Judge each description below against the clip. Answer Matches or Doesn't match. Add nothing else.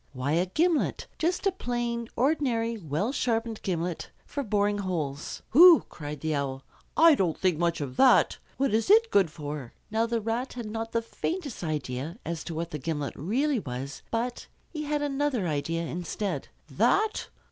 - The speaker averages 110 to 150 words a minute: Doesn't match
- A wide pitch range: Matches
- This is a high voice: Matches